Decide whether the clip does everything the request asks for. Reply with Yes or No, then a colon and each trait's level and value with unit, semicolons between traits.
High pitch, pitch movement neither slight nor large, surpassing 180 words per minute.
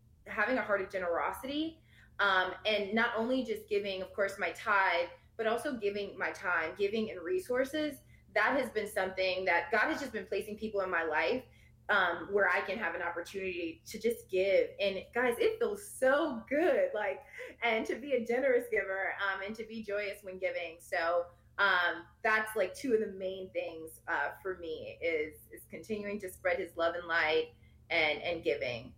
Yes: high, 205 Hz; average, 4.9 semitones; average, 190 wpm